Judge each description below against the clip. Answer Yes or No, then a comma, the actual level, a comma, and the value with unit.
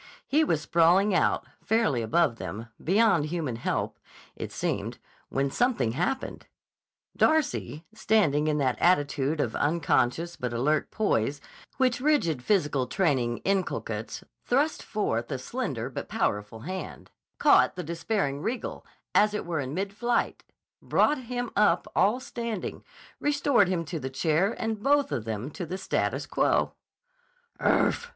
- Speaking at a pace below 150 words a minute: Yes, average, 140 wpm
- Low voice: No, medium, 170 Hz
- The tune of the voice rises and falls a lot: Yes, wide, 8.2 semitones